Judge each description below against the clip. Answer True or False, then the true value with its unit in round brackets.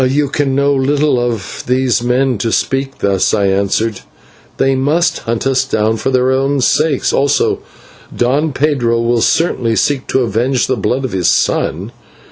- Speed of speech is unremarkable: True (165 wpm)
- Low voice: True (130 Hz)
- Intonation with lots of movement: False (2.9 semitones)